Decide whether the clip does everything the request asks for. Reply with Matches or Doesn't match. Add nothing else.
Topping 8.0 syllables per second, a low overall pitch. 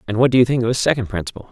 Matches